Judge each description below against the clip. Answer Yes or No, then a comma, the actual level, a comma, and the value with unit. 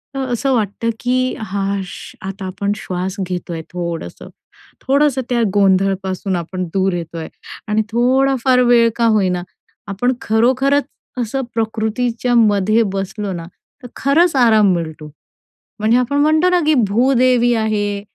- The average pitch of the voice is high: Yes, high, 220 Hz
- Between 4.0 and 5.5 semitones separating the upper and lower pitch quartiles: Yes, average, 4.7 semitones